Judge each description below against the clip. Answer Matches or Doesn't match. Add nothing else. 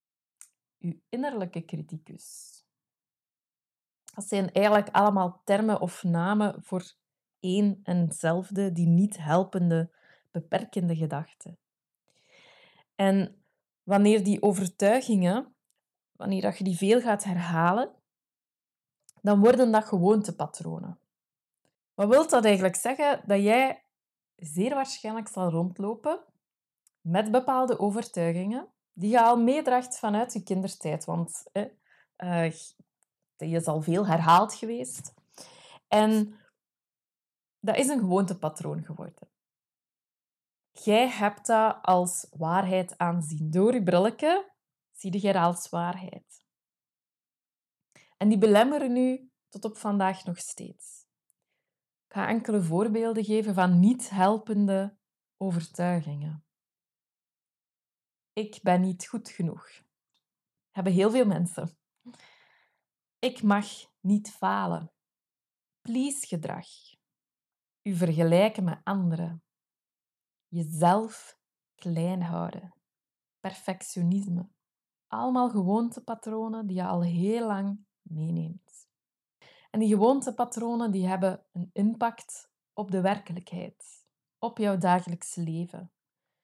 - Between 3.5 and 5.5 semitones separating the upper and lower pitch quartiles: Matches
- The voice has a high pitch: Matches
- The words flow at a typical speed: Doesn't match